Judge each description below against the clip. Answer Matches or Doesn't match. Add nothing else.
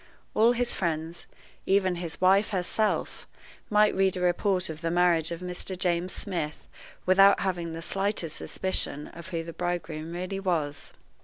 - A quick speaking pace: Doesn't match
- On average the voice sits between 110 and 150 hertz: Doesn't match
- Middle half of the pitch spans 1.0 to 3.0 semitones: Matches